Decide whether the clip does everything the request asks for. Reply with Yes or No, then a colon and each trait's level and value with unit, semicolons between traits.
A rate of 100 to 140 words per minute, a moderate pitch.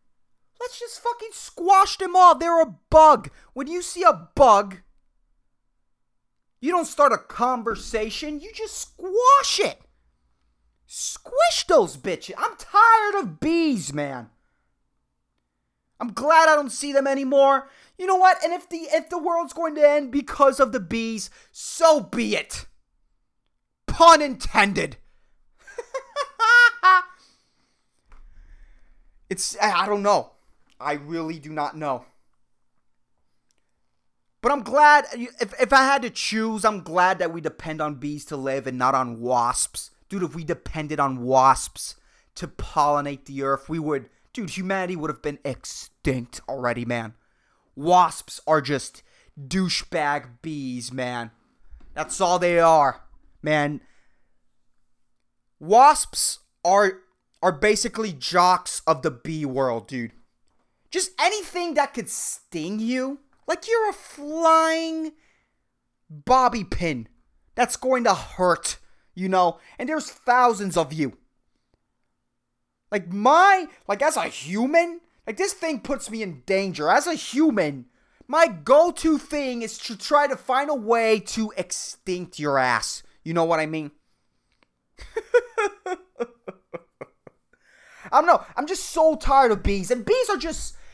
No: slow, 135 wpm; high, 230 Hz